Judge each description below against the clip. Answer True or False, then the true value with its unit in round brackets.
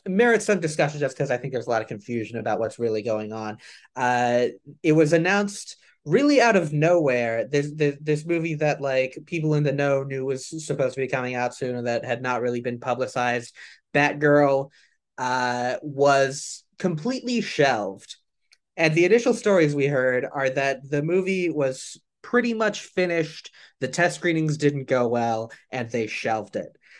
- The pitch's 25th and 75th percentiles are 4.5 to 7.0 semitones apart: True (5.1 semitones)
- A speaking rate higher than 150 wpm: True (175 wpm)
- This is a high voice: False (140 Hz)